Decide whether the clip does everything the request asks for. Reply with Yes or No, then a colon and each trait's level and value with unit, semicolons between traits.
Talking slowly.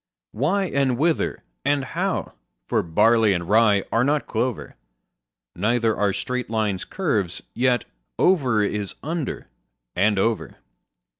Yes: slow, 125 wpm